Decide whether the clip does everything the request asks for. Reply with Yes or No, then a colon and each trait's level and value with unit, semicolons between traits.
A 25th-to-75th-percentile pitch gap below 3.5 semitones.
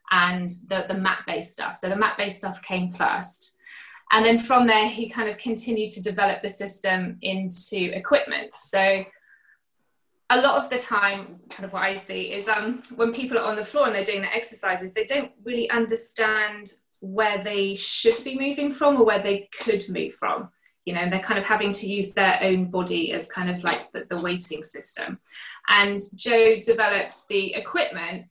Yes: average, 3.0 semitones